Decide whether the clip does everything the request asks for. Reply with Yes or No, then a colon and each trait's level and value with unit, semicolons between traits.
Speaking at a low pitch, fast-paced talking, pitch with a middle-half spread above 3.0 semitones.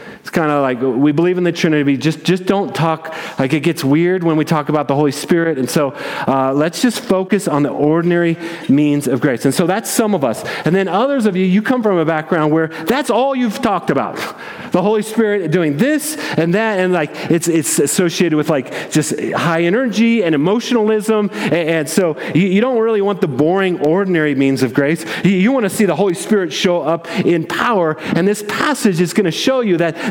No: medium, 175 Hz; fast, 215 wpm; average, 5.0 semitones